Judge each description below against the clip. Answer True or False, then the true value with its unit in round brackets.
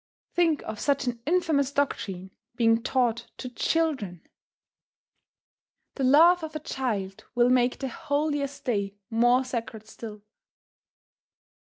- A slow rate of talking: True (120 wpm)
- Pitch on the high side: True (250 Hz)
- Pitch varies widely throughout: False (4.1 semitones)